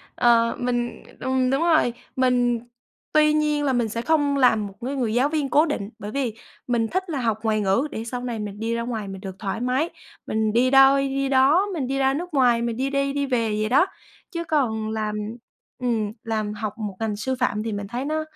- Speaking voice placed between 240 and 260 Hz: Yes, high, 245 Hz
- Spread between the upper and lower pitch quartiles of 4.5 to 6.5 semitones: No, average, 3.9 semitones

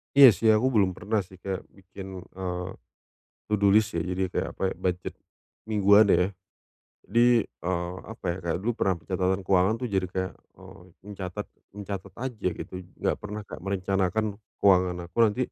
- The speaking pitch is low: Yes, very low, 95 Hz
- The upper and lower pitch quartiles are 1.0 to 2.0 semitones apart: No, narrow, 2.4 semitones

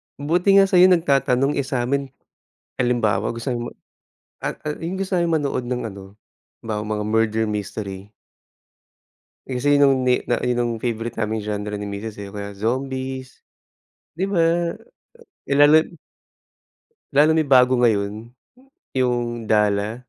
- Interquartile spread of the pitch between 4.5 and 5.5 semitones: Yes, average, 5.1 semitones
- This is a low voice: Yes, low, 125 Hz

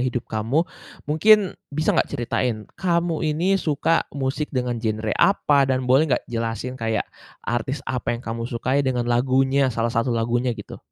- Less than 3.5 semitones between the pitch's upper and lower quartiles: No, average, 4.0 semitones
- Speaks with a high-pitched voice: No, low, 130 Hz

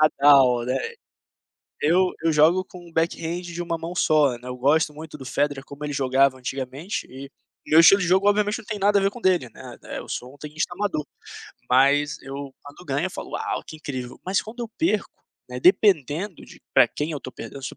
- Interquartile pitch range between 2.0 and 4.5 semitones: No, average, 4.9 semitones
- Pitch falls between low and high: Yes, medium, 155 Hz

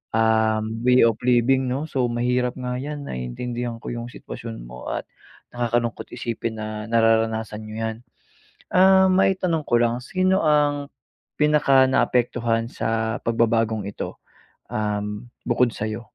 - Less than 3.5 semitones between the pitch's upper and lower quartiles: Yes, average, 2.7 semitones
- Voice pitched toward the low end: Yes, low, 120 Hz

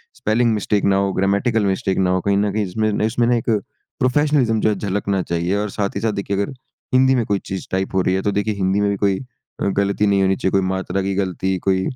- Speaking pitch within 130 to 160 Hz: No, low, 100 Hz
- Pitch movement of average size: No, narrow, 2.1 semitones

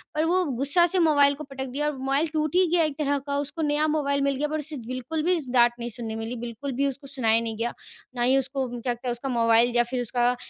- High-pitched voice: Yes, very high, 275 Hz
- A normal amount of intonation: Yes, average, 3.7 semitones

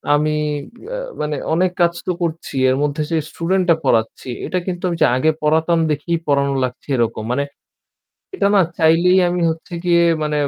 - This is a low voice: No, medium, 160 Hz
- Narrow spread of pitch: No, average, 3.2 semitones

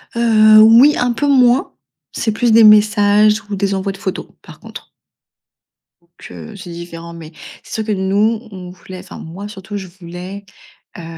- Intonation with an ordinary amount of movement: Yes, average, 3.2 semitones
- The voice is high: Yes, high, 200 Hz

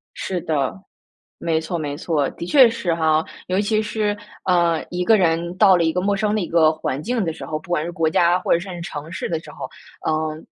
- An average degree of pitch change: Yes, average, 3.2 semitones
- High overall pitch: No, medium, 170 Hz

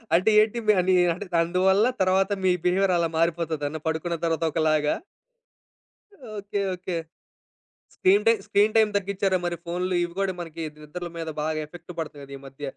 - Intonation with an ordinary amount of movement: Yes, average, 3.0 semitones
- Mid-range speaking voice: Yes, medium, 175 Hz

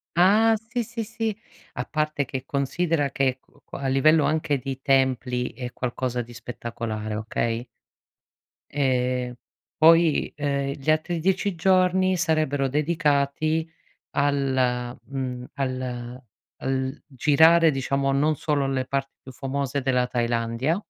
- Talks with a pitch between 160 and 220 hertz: No, medium, 140 Hz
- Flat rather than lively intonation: No, average, 3.7 semitones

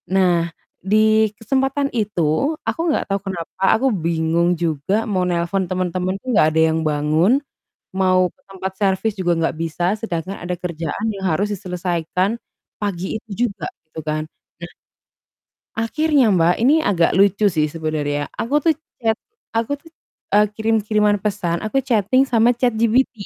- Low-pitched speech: No, high, 190 Hz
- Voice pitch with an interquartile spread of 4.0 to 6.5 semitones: Yes, average, 4.6 semitones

